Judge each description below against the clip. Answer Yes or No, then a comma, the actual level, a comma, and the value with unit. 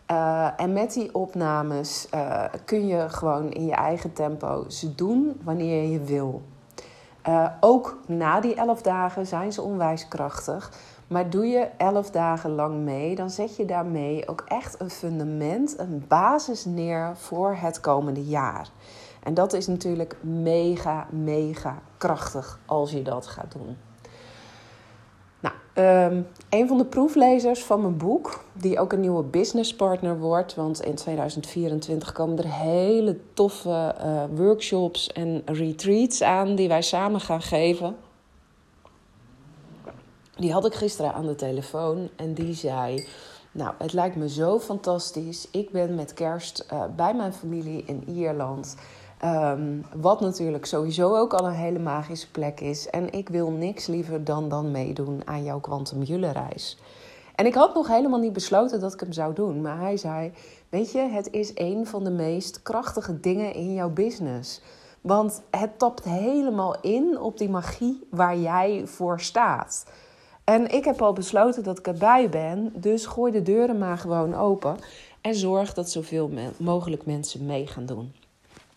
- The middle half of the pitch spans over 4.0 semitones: Yes, average, 4.7 semitones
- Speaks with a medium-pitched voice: Yes, medium, 170 Hz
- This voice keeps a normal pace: Yes, average, 160 wpm